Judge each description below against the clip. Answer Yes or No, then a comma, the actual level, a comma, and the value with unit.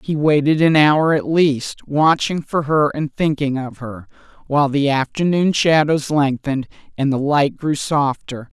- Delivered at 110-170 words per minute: Yes, average, 160 wpm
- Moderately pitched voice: Yes, medium, 145 Hz